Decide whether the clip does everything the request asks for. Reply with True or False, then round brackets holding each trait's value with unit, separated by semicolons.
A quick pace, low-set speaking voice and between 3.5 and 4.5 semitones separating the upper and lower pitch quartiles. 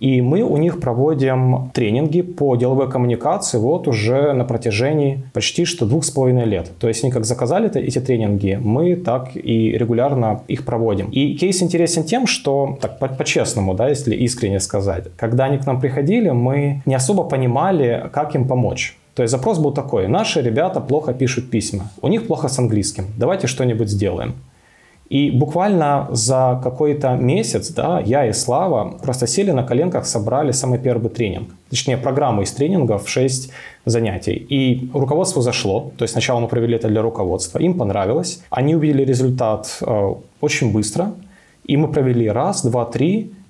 True (165 wpm; 130 Hz; 3.9 semitones)